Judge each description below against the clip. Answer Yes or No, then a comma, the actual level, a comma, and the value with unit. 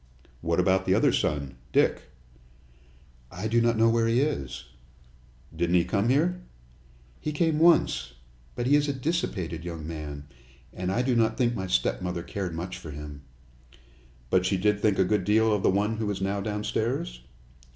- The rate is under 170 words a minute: No, average, 175 wpm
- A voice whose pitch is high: No, low, 100 Hz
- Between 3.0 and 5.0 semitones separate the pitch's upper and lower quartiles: No, wide, 5.4 semitones